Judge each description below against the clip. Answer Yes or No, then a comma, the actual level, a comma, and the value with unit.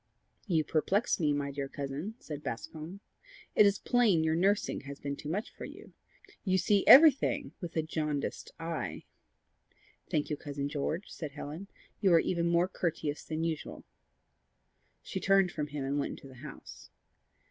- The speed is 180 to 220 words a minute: No, average, 165 wpm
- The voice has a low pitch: No, medium, 160 Hz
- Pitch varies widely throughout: No, average, 4.5 semitones